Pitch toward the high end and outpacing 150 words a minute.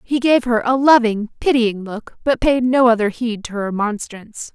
Yes: high, 235 Hz; average, 200 wpm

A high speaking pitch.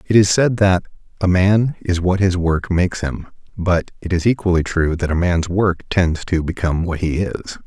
No: very low, 90 Hz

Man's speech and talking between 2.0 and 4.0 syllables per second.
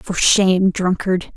No: female; 3.8 syllables/s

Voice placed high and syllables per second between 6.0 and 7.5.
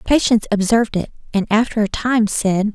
No: high, 215 Hz; 5.5 syllables/s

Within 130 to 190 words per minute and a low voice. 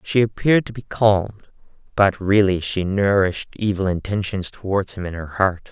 Yes: average, 170 wpm; low, 100 Hz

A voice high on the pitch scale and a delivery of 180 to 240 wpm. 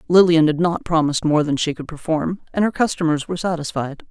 No: medium, 160 Hz; fast, 205 wpm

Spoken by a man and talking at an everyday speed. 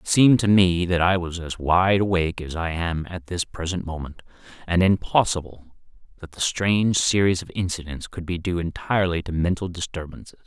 Yes: male; average, 185 wpm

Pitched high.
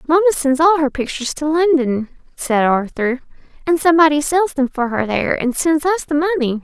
Yes: very high, 290 Hz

